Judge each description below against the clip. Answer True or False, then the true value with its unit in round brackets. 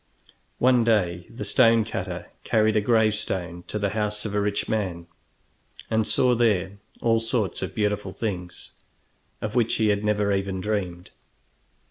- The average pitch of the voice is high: False (105 Hz)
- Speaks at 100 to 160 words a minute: True (150 wpm)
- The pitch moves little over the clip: True (2.3 semitones)